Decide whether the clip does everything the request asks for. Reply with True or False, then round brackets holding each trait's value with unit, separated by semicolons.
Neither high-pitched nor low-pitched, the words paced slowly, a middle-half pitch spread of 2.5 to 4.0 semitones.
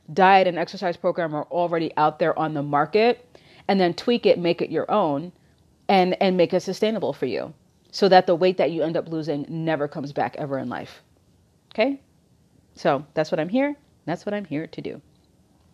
False (175 Hz; 200 wpm; 3.7 semitones)